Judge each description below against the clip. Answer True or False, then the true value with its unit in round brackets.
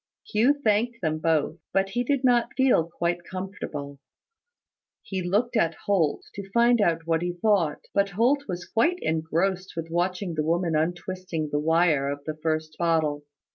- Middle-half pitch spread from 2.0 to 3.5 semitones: False (4.2 semitones)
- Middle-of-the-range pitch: True (175 Hz)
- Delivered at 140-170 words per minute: True (165 wpm)